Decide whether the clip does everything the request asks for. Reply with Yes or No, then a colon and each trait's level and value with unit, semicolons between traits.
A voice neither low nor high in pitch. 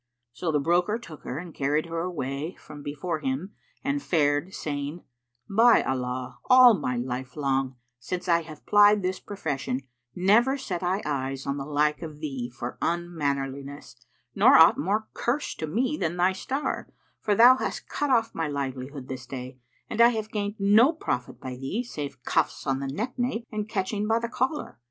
Yes: medium, 165 Hz